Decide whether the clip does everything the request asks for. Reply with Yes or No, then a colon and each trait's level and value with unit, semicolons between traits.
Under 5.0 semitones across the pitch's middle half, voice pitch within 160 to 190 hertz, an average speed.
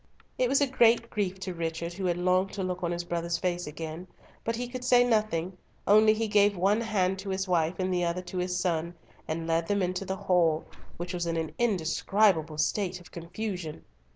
No: average, 3.3 semitones; medium, 185 Hz; fast, 210 wpm